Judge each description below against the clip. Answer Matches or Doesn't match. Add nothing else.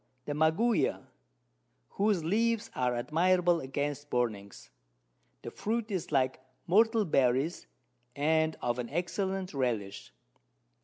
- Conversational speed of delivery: Doesn't match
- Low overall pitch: Doesn't match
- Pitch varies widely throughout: Matches